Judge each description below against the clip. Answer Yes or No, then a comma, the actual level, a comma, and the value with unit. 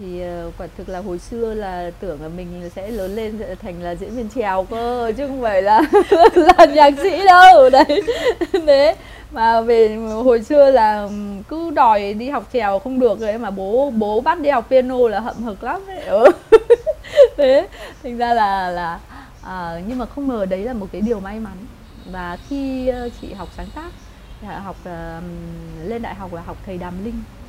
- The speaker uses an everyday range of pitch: No, wide, 6.4 semitones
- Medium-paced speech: Yes, average, 190 wpm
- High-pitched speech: Yes, high, 225 Hz